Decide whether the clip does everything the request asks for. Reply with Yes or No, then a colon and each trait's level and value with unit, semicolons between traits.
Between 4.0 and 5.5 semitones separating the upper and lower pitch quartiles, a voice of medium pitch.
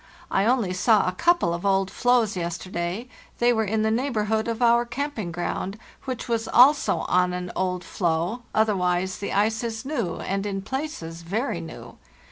No: average, 4.7 semitones; high, 210 Hz